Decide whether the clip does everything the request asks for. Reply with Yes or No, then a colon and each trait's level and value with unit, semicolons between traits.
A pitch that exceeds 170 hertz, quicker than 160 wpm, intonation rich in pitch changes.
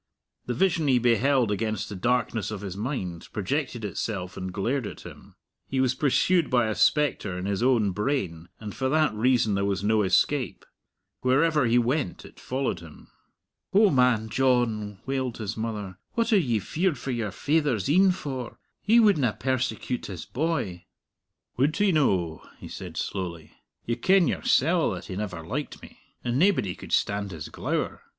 No: low, 120 Hz; average, 170 wpm; wide, 5.7 semitones